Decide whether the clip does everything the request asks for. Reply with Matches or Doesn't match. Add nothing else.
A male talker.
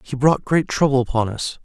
Matches